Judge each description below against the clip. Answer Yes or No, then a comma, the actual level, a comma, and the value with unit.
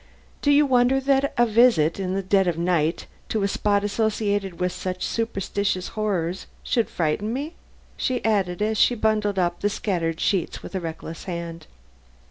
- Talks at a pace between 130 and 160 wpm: No, average, 170 wpm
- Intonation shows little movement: No, average, 3.9 semitones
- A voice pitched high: Yes, high, 200 Hz